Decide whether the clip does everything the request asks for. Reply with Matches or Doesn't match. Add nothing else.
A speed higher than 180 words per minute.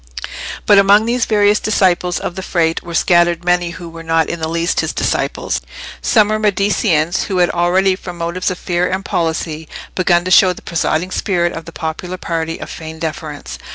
Matches